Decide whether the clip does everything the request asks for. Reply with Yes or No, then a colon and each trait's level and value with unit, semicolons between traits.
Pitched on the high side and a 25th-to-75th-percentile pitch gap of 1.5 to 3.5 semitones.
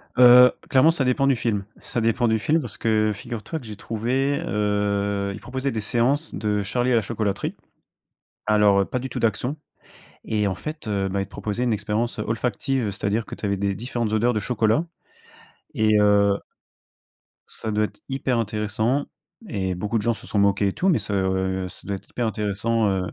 No: low, 110 Hz; average, 3.2 semitones